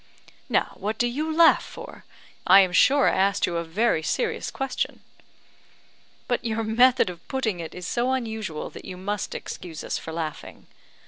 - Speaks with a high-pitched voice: Yes, high, 215 Hz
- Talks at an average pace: Yes, average, 175 wpm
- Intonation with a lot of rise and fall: Yes, wide, 5.8 semitones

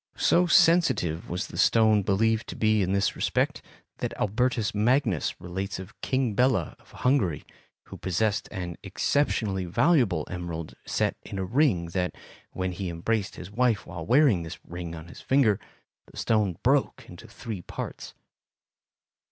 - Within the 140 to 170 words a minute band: Yes, average, 150 wpm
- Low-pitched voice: Yes, low, 100 Hz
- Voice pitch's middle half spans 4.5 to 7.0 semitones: Yes, average, 4.9 semitones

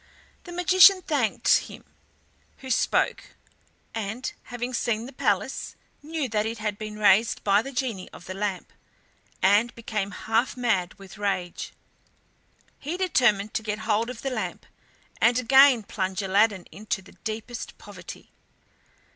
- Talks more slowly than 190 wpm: Yes, average, 140 wpm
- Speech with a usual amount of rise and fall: Yes, average, 3.8 semitones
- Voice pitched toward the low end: No, high, 220 Hz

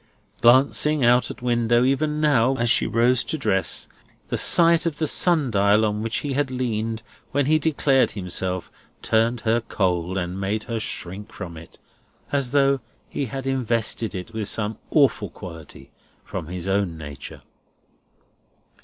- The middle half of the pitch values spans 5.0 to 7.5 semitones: Yes, wide, 5.5 semitones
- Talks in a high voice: No, low, 115 Hz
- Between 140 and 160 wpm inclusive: Yes, average, 155 wpm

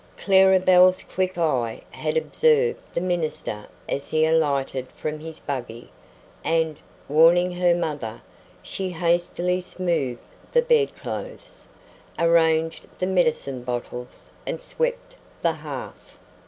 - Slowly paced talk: Yes, slow, 115 wpm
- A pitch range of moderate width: Yes, average, 3.9 semitones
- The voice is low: No, medium, 170 Hz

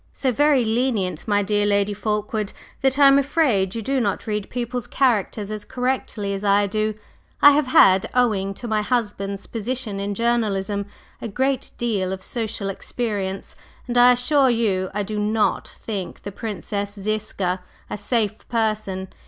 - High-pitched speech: Yes, high, 215 Hz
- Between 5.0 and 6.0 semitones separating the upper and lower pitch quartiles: No, average, 3.4 semitones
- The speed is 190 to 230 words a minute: No, average, 160 wpm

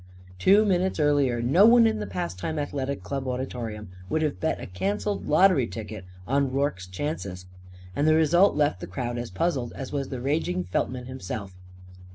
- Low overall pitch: Yes, low, 130 Hz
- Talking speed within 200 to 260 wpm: No, average, 175 wpm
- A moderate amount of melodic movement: No, wide, 6.7 semitones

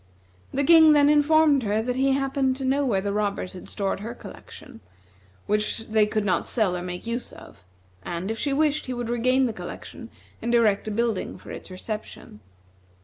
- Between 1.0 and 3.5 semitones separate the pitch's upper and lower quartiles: No, average, 4.7 semitones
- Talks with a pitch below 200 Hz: No, high, 235 Hz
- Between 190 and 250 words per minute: Yes, average, 195 wpm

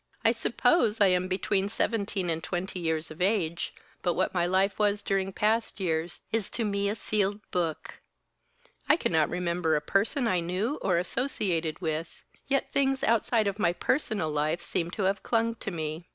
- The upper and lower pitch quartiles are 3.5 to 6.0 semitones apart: Yes, average, 3.8 semitones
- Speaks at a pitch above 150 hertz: Yes, high, 190 Hz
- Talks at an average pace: Yes, average, 180 wpm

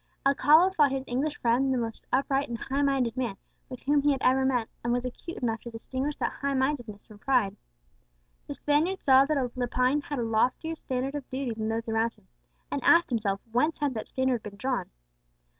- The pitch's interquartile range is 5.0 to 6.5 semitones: No, average, 3.2 semitones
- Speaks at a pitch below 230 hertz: No, very high, 260 Hz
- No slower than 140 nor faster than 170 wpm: No, average, 195 wpm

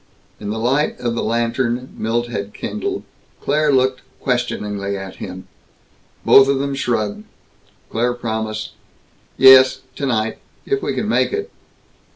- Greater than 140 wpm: No, slow, 135 wpm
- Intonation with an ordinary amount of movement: Yes, average, 3.6 semitones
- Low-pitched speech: Yes, low, 120 Hz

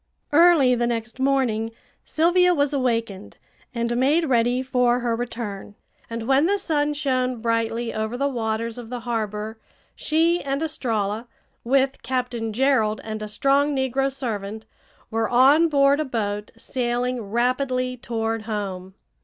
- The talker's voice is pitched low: No, high, 245 Hz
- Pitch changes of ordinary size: Yes, average, 3.4 semitones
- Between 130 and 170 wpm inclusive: Yes, average, 140 wpm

